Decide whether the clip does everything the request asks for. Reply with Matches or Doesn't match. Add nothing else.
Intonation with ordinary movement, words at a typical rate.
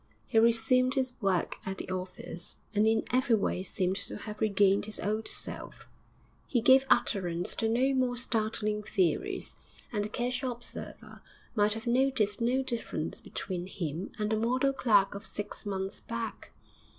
Matches